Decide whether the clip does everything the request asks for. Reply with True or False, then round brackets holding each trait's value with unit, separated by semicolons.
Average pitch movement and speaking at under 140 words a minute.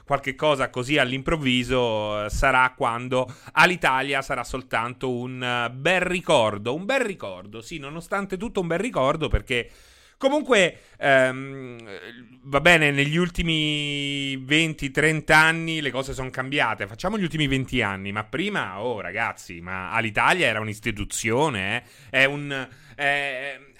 True (3.8 semitones; 130 wpm)